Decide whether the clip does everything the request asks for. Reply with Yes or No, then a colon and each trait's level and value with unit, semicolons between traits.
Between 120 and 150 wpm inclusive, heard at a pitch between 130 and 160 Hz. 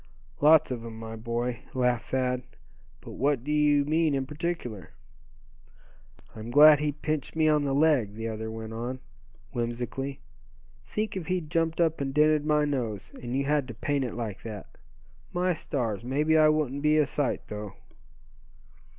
No: average, 165 wpm; medium, 140 Hz